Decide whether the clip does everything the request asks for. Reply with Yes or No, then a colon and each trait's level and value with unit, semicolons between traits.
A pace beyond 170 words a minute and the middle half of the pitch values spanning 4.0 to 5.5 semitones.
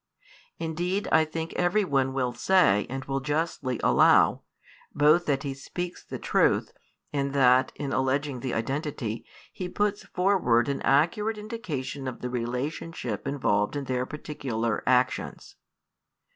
No: slow, 135 wpm; average, 4.4 semitones